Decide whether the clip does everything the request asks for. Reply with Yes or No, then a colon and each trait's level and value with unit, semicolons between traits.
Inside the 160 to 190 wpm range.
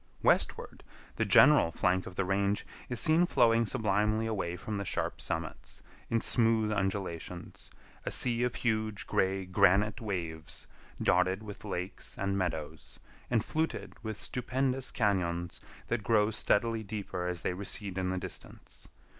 No: average, 145 wpm